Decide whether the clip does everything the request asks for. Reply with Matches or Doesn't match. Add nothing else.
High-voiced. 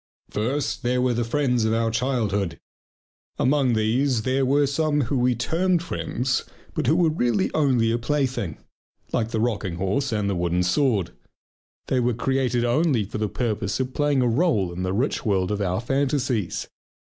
Doesn't match